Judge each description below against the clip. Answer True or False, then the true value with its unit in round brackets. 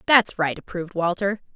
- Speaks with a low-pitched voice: False (185 Hz)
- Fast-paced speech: False (155 wpm)